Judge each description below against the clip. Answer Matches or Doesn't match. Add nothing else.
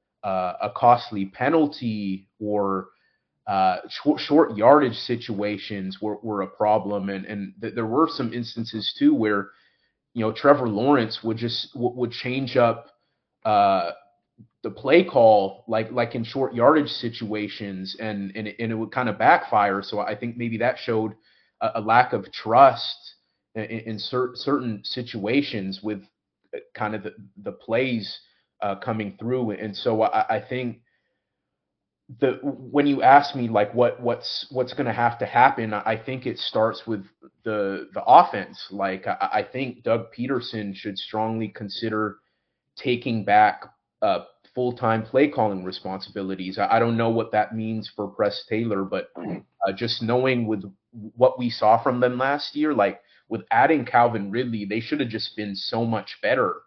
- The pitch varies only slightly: Doesn't match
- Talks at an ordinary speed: Matches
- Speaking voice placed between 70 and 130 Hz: Matches